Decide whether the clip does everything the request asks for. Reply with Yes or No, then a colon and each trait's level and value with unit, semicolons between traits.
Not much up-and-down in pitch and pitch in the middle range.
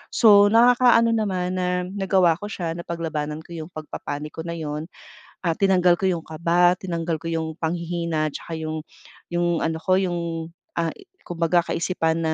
Yes: narrow, 2.2 semitones; medium, 170 Hz